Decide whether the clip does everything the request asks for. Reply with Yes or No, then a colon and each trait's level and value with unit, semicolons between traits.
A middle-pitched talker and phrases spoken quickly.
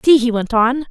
No: high, 245 Hz; fast, 265 wpm